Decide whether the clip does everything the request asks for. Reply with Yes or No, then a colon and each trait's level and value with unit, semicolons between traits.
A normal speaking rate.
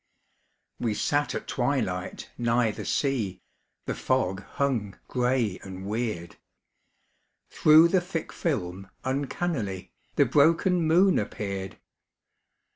No: slow, 105 wpm